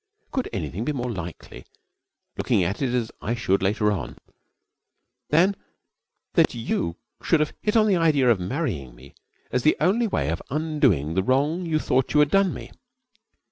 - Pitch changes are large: Yes, wide, 8.7 semitones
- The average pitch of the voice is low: Yes, low, 125 Hz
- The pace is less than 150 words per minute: No, average, 175 wpm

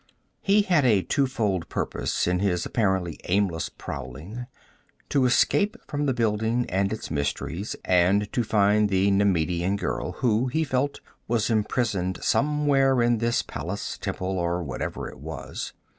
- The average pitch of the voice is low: Yes, low, 105 Hz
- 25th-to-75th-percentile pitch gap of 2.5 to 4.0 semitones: No, average, 5.3 semitones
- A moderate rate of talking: Yes, average, 145 wpm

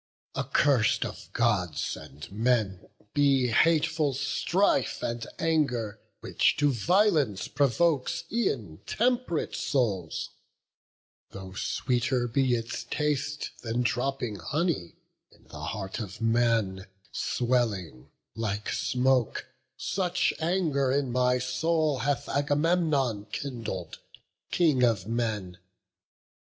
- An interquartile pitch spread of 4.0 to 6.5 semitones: Yes, average, 5.2 semitones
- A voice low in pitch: Yes, low, 125 Hz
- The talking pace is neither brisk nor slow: No, slow, 100 wpm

